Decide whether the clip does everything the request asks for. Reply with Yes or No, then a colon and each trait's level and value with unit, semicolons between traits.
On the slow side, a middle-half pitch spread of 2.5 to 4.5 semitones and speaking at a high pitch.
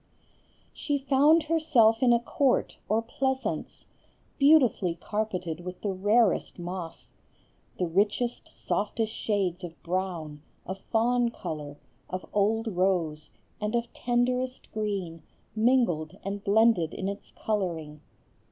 No: slow, 115 wpm; average, 5.0 semitones; high, 205 Hz